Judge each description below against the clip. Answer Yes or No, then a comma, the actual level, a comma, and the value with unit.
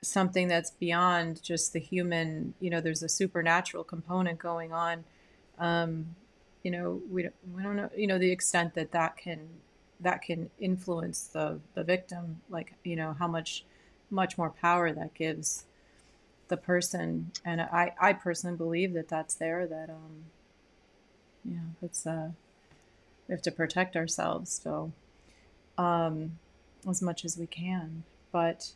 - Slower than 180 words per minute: Yes, average, 150 wpm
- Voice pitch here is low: No, medium, 170 Hz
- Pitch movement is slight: Yes, narrow, 1.7 semitones